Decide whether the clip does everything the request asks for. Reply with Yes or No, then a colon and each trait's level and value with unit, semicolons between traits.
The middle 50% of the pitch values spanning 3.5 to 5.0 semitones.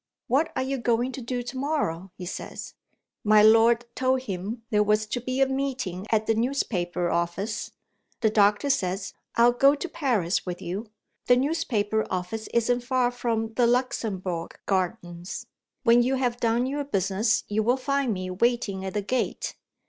Yes: average, 4.5 semitones